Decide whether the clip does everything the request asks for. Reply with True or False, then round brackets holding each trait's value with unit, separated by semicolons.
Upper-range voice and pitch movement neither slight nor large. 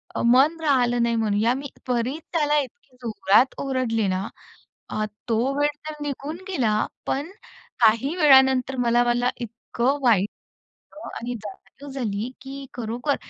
True (250 Hz; 3.3 semitones)